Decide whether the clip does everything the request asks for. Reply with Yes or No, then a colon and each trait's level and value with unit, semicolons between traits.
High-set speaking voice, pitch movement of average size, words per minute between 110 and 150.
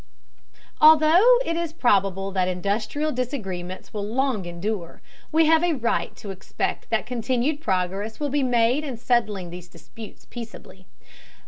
No: high, 230 Hz; wide, 7.1 semitones; average, 140 wpm